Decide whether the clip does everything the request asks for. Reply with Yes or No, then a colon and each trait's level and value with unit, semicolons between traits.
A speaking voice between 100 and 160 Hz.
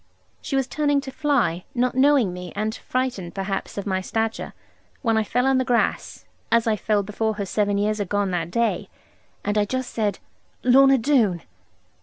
No: high, 220 Hz